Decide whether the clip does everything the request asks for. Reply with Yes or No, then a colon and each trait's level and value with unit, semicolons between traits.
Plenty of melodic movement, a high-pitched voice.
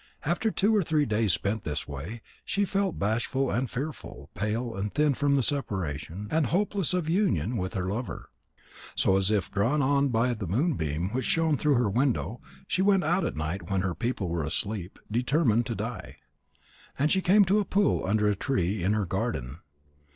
No: wide, 7.7 semitones; low, 120 Hz